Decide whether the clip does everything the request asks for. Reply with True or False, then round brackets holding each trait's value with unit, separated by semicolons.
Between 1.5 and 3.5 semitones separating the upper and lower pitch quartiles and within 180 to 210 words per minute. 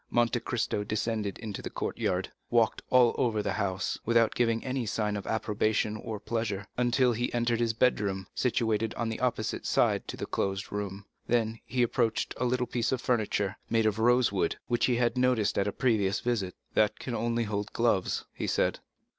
True (2.5 semitones; 190 wpm)